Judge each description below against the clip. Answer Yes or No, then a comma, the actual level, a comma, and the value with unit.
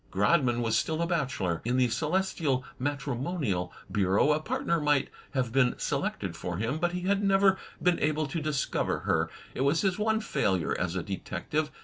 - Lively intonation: Yes, wide, 6.4 semitones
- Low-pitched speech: No, medium, 145 Hz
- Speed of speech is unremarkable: Yes, average, 190 wpm